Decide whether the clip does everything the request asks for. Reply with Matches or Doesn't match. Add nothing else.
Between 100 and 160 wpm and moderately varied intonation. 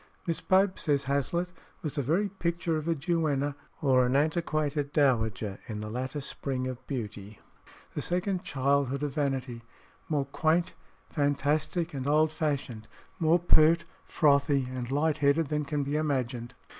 Matches